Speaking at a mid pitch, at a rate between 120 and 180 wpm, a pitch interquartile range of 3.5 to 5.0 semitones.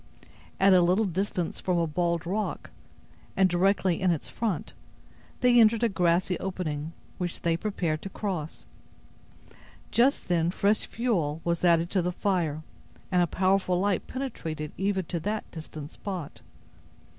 No: medium, 180 Hz; average, 145 wpm; average, 2.9 semitones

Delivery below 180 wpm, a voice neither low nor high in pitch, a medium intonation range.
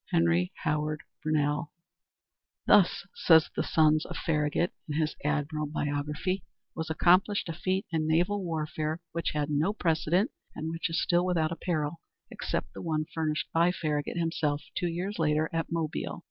No: average, 160 wpm; medium, 160 Hz; narrow, 2.1 semitones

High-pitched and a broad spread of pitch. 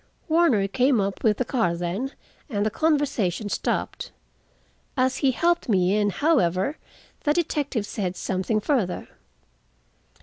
Yes: high, 225 Hz; wide, 6.6 semitones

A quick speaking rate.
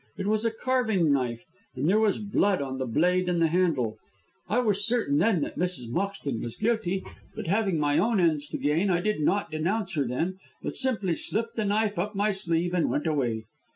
Yes: fast, 210 wpm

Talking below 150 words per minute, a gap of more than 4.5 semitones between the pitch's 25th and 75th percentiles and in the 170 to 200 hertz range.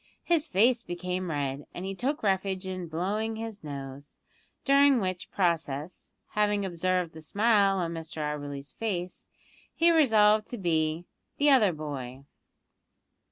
Yes: slow, 135 wpm; average, 5.2 semitones; medium, 185 Hz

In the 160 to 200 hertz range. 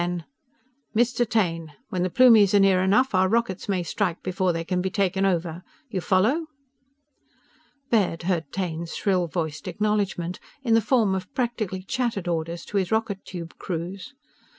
Yes: high, 190 Hz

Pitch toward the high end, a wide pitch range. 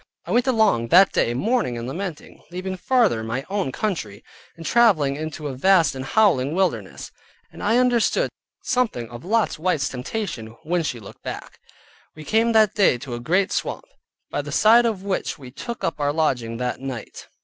No: medium, 165 Hz; wide, 8.9 semitones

